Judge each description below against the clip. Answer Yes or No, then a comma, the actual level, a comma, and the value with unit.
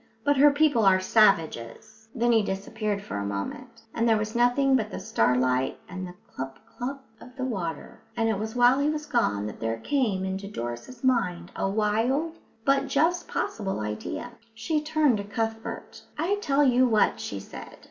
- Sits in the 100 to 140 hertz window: No, high, 225 Hz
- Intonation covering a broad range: Yes, wide, 6.0 semitones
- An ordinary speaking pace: Yes, average, 180 wpm